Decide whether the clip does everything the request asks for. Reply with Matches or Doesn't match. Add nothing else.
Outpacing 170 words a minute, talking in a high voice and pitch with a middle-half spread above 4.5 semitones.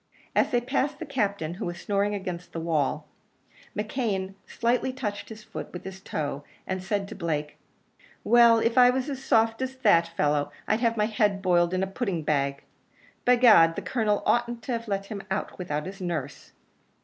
Matches